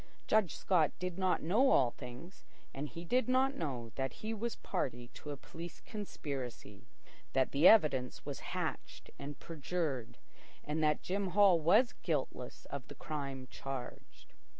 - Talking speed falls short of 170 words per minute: Yes, average, 150 wpm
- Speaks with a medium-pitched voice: Yes, medium, 155 Hz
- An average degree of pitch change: No, wide, 5.9 semitones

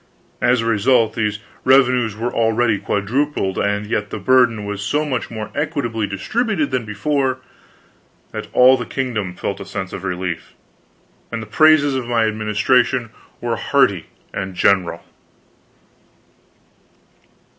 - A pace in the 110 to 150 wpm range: Yes, slow, 135 wpm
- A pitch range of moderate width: Yes, average, 4.1 semitones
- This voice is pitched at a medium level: No, low, 115 Hz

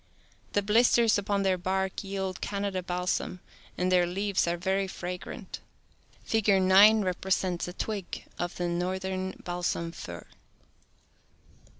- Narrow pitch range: Yes, narrow, 1.9 semitones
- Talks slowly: Yes, slow, 125 wpm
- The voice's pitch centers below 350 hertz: Yes, high, 190 Hz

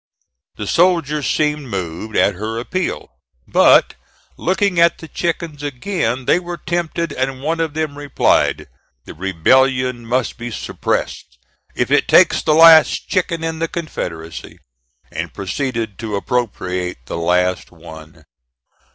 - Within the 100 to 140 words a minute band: Yes, slow, 135 wpm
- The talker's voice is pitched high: No, low, 130 Hz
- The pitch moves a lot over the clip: Yes, wide, 8.7 semitones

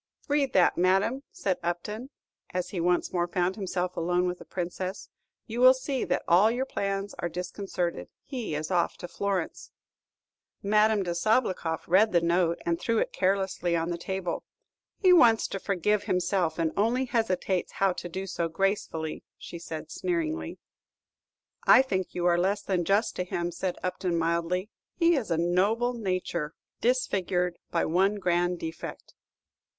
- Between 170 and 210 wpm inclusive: No, average, 160 wpm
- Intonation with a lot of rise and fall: No, average, 3.2 semitones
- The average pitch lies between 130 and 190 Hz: Yes, medium, 185 Hz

